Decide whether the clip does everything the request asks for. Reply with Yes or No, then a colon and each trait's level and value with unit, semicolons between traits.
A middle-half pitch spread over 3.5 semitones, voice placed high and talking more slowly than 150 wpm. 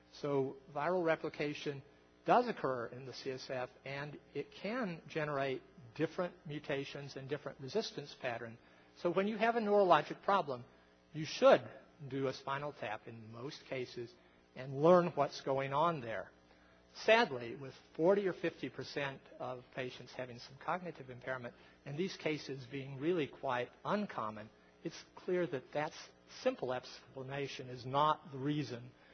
No: average, 4.0 semitones; medium, 140 Hz; average, 140 wpm